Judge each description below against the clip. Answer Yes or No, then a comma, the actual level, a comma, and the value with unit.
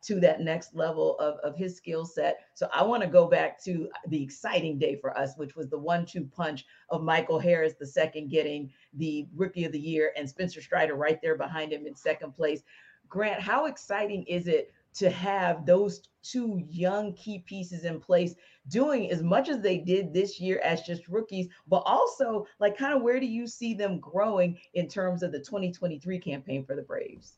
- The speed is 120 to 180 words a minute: No, fast, 205 wpm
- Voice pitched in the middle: Yes, medium, 175 Hz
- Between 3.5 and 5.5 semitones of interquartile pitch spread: Yes, average, 4.1 semitones